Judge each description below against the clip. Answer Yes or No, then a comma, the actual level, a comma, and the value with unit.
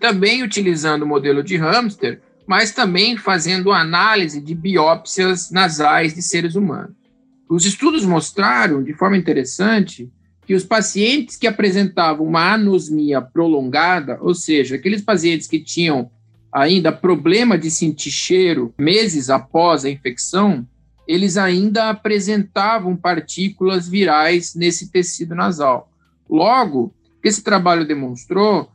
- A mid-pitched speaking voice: Yes, medium, 180 Hz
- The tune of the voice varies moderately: Yes, average, 4.5 semitones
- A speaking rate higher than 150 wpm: No, slow, 120 wpm